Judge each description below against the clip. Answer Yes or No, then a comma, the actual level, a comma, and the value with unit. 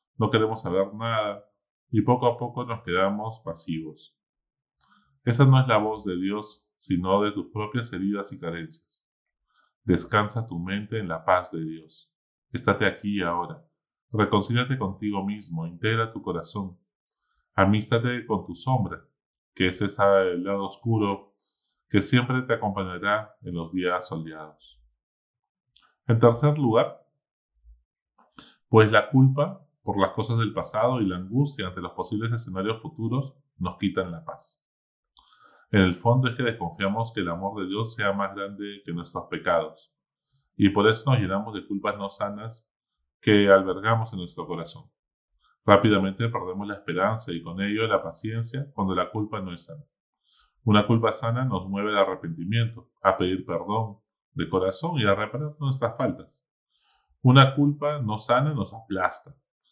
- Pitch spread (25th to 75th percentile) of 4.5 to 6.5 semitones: No, average, 3.9 semitones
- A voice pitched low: Yes, low, 105 Hz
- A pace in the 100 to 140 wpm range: No, average, 155 wpm